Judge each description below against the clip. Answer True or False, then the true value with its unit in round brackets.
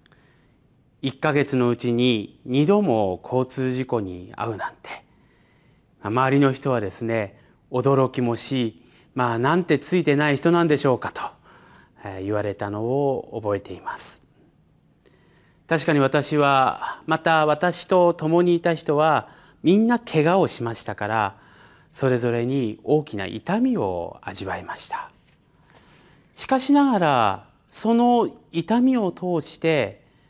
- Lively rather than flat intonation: True (5.9 semitones)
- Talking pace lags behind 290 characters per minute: True (235 characters per minute)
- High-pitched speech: False (135 Hz)